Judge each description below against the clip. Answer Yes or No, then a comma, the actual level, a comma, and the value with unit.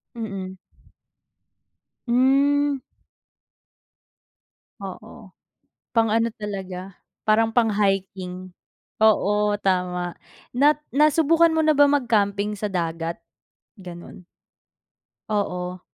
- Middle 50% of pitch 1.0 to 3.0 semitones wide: No, average, 5.2 semitones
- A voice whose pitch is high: Yes, high, 210 Hz